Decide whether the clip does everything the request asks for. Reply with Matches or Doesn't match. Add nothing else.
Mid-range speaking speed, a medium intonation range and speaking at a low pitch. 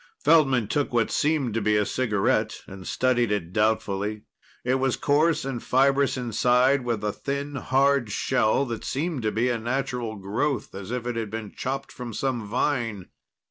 Matches